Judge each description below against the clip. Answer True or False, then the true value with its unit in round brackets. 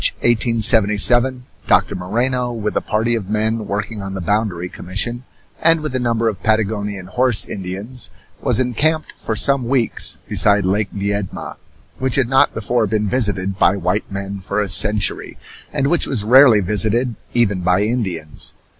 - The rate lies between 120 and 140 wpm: False (165 wpm)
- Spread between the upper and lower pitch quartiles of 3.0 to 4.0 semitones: True (3.4 semitones)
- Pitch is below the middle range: True (110 Hz)